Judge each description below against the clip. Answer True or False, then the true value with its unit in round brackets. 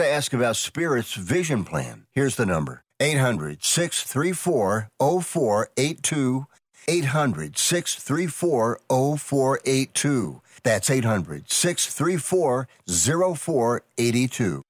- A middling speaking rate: False (55 wpm)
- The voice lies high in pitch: False (135 Hz)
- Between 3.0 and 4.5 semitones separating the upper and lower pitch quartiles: False (5.0 semitones)